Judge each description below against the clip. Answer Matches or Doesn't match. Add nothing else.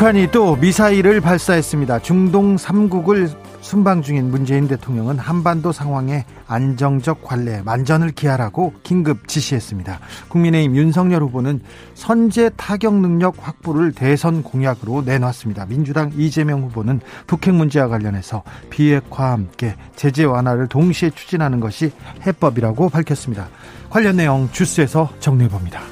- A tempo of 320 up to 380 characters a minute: Matches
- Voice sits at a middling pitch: Matches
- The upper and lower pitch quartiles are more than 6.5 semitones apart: Doesn't match